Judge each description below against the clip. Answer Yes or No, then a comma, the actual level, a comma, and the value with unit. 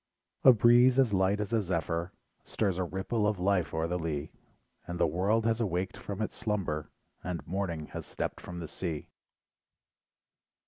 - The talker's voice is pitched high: No, very low, 95 Hz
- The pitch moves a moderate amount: Yes, average, 4.0 semitones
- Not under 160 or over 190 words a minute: Yes, average, 170 wpm